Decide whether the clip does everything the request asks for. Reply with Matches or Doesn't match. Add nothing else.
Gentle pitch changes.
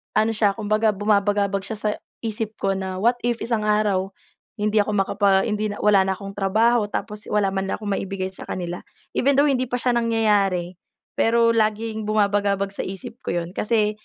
Matches